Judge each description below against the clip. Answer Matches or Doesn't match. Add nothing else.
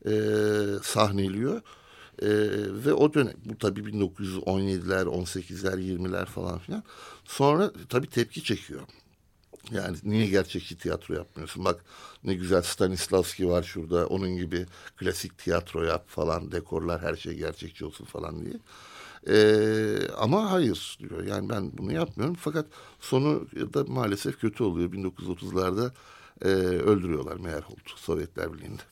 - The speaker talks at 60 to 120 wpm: Doesn't match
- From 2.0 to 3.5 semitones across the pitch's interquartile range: Matches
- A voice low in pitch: Matches